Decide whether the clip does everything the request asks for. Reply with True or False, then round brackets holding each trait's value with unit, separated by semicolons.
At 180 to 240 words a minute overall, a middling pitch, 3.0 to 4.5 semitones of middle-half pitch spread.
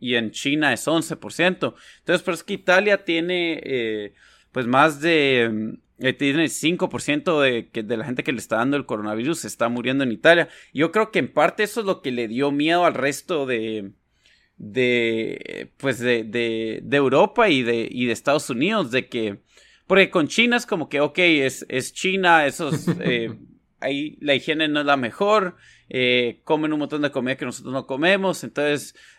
False (190 wpm; 145 Hz; 5.5 semitones)